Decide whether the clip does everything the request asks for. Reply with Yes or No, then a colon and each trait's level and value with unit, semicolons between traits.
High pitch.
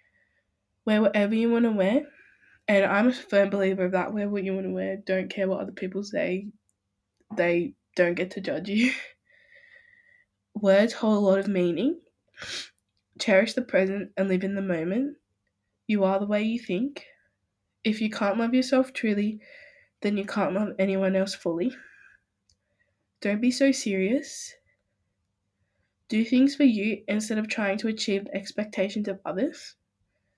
Yes: high, 205 Hz